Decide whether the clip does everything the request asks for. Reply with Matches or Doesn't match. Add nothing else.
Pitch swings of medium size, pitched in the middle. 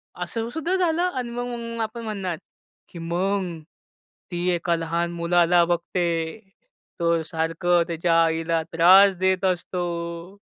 Matches